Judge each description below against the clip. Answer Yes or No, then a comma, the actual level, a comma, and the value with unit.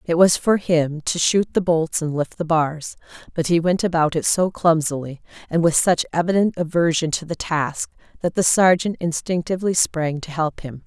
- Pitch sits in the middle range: Yes, medium, 165 Hz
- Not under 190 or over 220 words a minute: Yes, average, 195 wpm